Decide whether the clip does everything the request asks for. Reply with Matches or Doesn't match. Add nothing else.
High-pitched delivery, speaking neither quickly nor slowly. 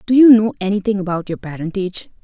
Matches